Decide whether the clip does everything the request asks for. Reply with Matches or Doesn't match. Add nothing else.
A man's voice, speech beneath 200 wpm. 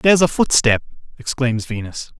Matches